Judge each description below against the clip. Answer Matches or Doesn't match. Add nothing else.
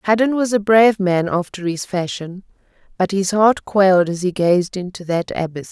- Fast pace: Doesn't match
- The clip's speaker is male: Doesn't match